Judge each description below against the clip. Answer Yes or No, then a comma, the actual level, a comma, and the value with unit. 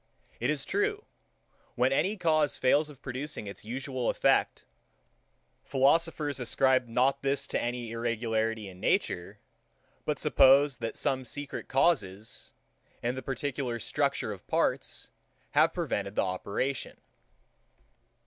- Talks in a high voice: No, low, 130 Hz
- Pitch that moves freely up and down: No, average, 3.5 semitones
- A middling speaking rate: No, slow, 120 wpm